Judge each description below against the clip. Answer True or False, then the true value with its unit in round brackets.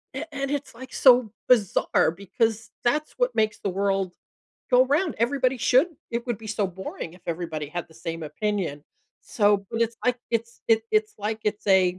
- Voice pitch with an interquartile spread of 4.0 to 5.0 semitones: True (4.6 semitones)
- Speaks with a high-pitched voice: True (215 Hz)